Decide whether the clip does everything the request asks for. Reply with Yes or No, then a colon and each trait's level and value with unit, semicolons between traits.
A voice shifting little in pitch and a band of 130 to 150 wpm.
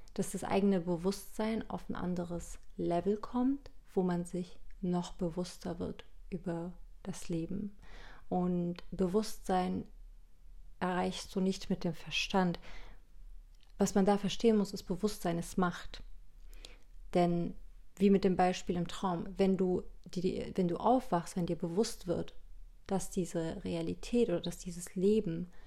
Yes: narrow, 2.3 semitones; average, 140 wpm